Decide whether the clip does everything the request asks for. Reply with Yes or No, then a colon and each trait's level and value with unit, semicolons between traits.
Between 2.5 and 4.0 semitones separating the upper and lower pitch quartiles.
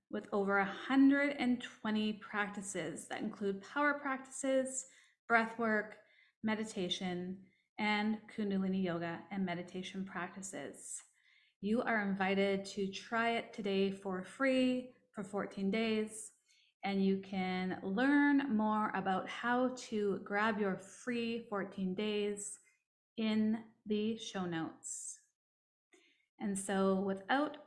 Yes: average, 3.4 semitones